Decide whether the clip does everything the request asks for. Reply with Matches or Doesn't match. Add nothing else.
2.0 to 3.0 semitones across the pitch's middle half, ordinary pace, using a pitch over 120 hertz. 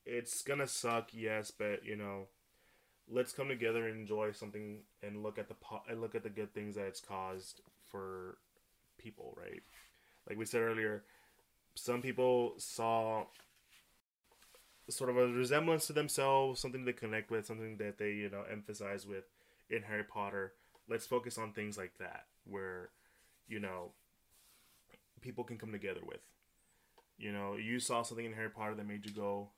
Doesn't match